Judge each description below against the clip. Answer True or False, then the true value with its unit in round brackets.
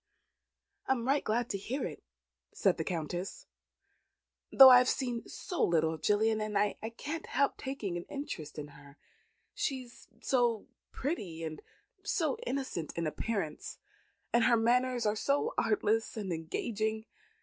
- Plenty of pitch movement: True (6.8 semitones)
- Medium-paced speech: True (150 wpm)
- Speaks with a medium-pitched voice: False (220 Hz)